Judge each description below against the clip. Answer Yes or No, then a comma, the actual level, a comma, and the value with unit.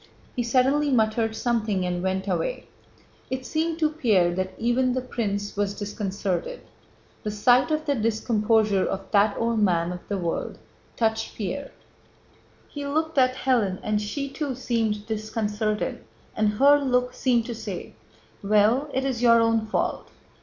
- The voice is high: Yes, high, 225 Hz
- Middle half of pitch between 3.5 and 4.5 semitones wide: Yes, average, 3.9 semitones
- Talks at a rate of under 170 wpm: Yes, average, 155 wpm